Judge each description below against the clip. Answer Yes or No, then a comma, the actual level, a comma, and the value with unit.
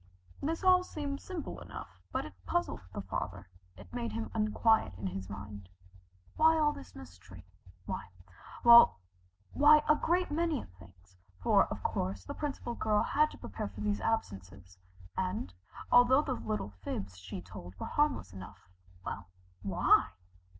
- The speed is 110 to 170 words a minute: Yes, average, 150 wpm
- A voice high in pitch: No, low, 105 Hz